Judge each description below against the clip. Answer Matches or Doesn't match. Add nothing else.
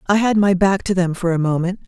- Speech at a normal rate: Doesn't match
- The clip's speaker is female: Matches